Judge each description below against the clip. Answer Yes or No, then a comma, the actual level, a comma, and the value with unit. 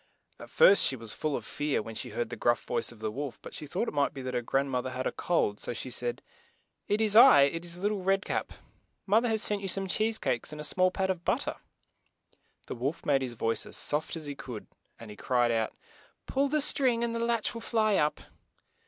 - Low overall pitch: No, medium, 150 Hz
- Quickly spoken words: Yes, fast, 255 wpm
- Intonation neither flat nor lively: No, wide, 8.6 semitones